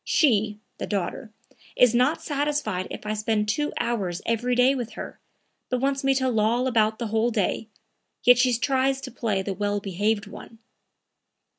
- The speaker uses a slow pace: No, average, 170 wpm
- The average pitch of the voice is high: Yes, high, 230 Hz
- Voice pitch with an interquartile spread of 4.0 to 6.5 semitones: No, average, 3.6 semitones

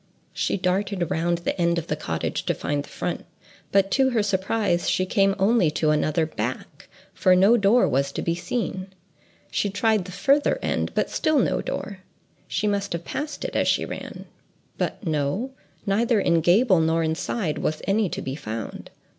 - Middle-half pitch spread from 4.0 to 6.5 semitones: Yes, average, 4.6 semitones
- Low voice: No, medium, 185 Hz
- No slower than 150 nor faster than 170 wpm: No, average, 180 wpm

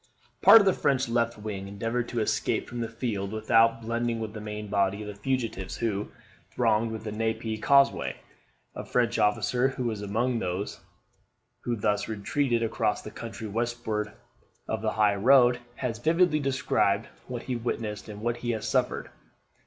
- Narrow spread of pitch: Yes, narrow, 2.3 semitones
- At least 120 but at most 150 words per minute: No, average, 165 wpm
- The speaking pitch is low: Yes, low, 115 Hz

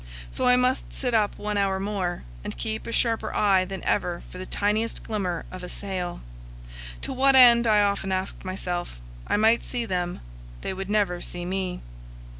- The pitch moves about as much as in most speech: Yes, average, 3.4 semitones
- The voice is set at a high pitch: Yes, high, 195 Hz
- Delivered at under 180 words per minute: No, average, 185 wpm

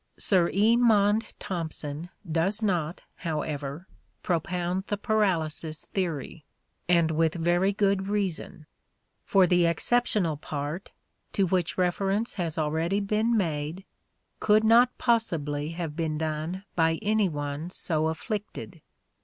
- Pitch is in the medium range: Yes, medium, 175 Hz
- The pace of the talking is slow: Yes, slow, 120 wpm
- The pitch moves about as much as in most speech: Yes, average, 4.1 semitones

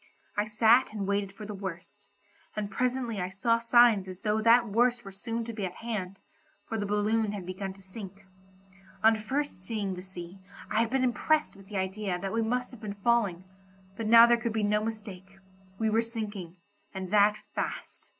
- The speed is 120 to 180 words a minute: No, average, 200 wpm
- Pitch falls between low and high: No, high, 210 Hz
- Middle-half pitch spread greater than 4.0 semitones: No, average, 3.0 semitones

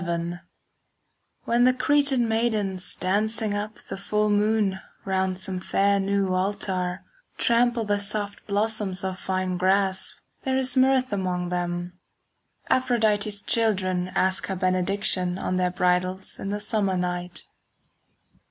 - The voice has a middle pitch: No, high, 195 Hz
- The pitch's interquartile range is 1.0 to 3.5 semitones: Yes, average, 2.8 semitones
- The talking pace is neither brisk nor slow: No, slow, 130 wpm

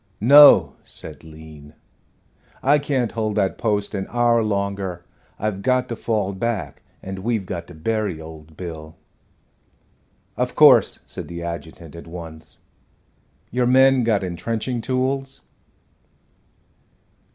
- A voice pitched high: No, low, 100 Hz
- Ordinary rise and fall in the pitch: No, wide, 5.9 semitones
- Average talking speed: No, slow, 120 wpm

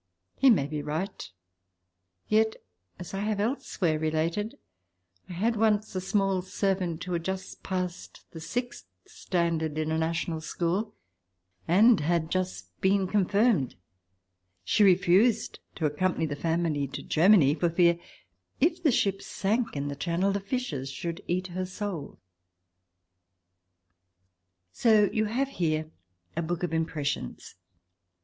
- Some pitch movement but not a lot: Yes, average, 4.3 semitones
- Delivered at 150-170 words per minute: No, slow, 135 wpm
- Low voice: No, medium, 180 Hz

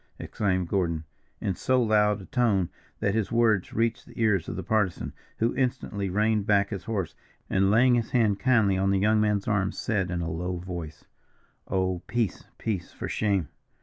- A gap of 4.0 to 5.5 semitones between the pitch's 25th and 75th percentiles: No, average, 3.1 semitones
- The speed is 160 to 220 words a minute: Yes, average, 180 wpm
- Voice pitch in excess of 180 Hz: No, low, 100 Hz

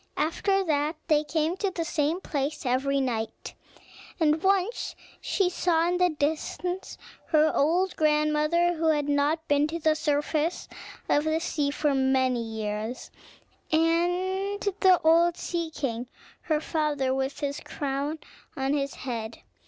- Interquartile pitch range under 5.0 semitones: Yes, average, 3.2 semitones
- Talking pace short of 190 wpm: Yes, average, 140 wpm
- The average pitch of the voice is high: Yes, very high, 305 Hz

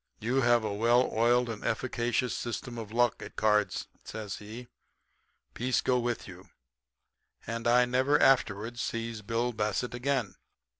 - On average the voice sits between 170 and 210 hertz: No, low, 120 Hz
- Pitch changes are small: Yes, narrow, 2.0 semitones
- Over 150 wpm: No, average, 145 wpm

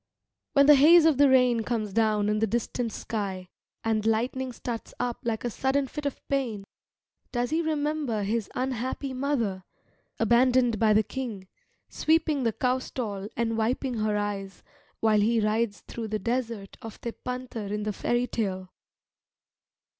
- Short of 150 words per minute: No, average, 155 wpm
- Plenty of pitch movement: No, average, 3.4 semitones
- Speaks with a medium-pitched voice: No, high, 235 Hz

